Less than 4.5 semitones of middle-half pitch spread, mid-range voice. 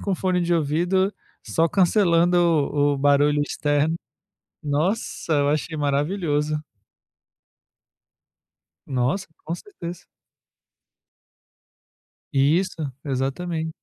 Yes: average, 3.4 semitones; medium, 160 Hz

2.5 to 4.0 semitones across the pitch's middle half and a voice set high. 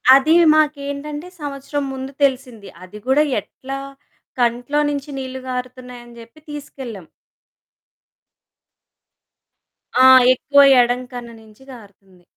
Yes: average, 2.9 semitones; very high, 260 Hz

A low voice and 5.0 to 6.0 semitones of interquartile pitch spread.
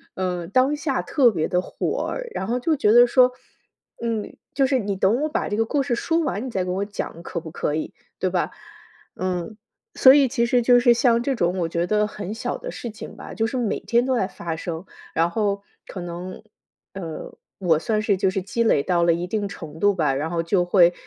No: high, 205 Hz; wide, 5.5 semitones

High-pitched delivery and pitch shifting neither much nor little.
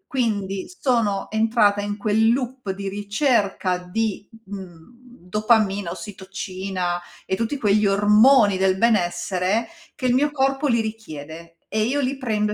Yes: high, 210 Hz; average, 3.4 semitones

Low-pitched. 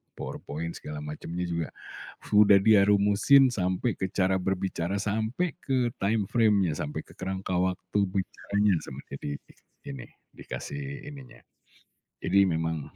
Yes: very low, 95 Hz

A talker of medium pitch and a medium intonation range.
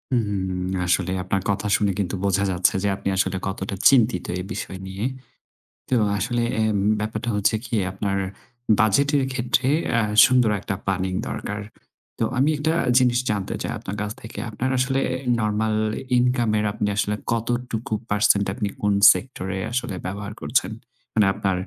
No: low, 105 Hz; average, 3.6 semitones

